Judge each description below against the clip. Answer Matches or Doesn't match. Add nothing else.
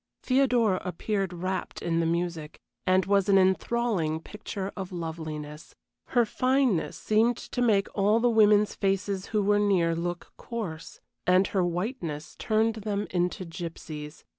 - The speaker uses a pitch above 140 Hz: Matches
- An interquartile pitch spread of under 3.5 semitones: Doesn't match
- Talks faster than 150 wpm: Doesn't match